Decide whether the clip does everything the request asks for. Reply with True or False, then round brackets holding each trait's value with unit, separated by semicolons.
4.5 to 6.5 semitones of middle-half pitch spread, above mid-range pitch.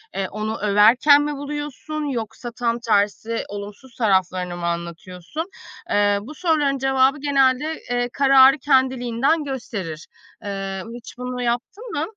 True (5.2 semitones; 245 Hz)